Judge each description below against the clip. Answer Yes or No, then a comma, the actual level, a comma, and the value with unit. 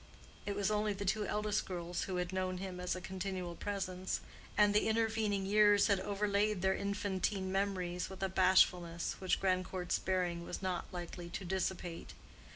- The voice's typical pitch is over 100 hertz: Yes, high, 190 Hz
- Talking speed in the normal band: Yes, average, 165 wpm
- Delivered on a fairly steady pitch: Yes, narrow, 2.0 semitones